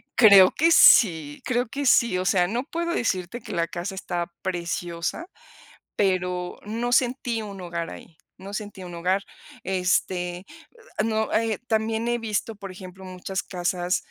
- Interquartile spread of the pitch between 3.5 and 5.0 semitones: Yes, average, 4.0 semitones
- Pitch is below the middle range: No, high, 190 Hz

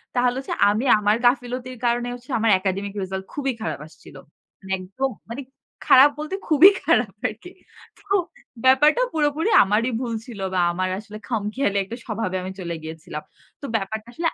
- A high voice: Yes, high, 230 Hz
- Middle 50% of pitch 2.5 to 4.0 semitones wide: No, average, 5.3 semitones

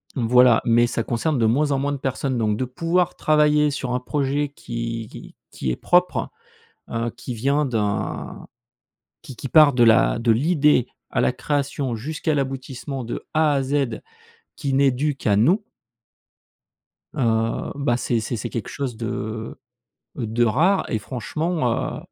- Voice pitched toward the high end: No, low, 130 Hz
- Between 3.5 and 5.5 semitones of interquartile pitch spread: Yes, average, 4.0 semitones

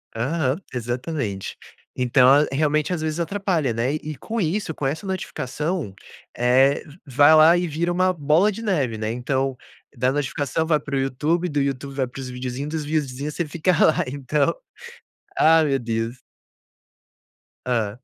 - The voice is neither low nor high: Yes, medium, 145 Hz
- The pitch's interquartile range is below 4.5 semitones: Yes, average, 4.0 semitones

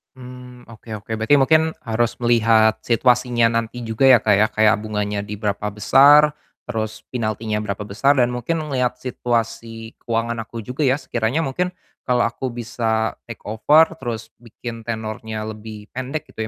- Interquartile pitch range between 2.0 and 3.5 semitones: Yes, narrow, 2.5 semitones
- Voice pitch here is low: Yes, low, 115 Hz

